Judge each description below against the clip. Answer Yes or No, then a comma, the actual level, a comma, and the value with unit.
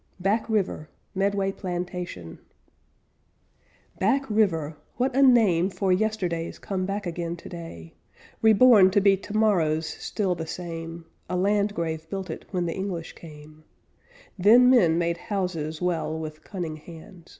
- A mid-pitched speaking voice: Yes, medium, 180 Hz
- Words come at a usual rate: No, slow, 130 wpm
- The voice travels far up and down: No, average, 3.6 semitones